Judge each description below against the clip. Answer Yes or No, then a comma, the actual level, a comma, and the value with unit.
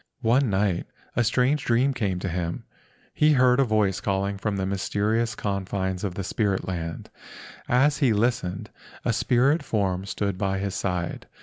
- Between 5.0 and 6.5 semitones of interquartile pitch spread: No, average, 4.2 semitones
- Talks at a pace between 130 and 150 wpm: No, average, 170 wpm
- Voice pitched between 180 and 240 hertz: No, low, 100 Hz